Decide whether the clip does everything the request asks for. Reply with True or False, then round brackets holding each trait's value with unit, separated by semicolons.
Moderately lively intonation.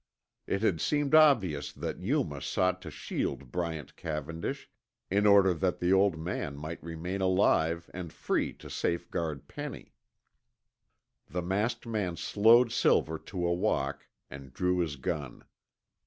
True (3.8 semitones)